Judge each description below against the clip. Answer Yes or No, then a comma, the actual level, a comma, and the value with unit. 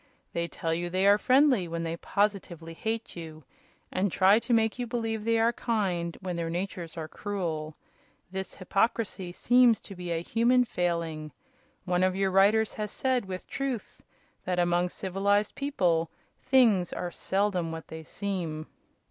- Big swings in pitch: No, average, 4.5 semitones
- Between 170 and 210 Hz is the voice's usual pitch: Yes, high, 190 Hz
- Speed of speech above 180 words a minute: No, average, 160 wpm